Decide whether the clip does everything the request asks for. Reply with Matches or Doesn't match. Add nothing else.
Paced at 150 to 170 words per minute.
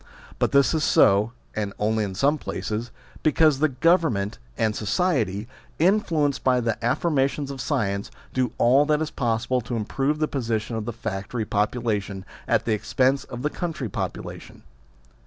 Matches